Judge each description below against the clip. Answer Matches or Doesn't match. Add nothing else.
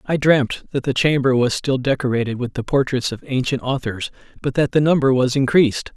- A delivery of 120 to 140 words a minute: Doesn't match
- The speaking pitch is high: Doesn't match